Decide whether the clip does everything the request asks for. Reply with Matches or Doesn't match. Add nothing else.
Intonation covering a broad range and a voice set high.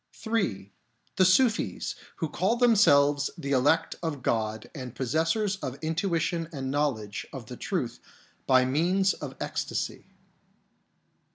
Doesn't match